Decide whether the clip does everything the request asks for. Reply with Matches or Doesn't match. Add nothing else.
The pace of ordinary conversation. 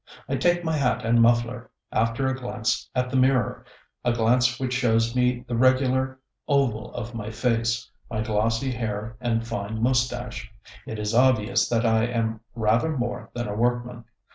Matches